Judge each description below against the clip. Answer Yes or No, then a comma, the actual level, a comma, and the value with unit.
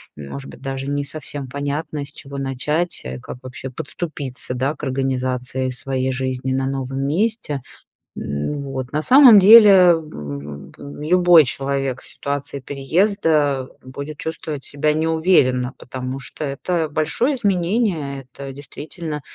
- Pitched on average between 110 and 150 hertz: Yes, medium, 140 Hz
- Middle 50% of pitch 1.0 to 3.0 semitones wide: No, average, 3.4 semitones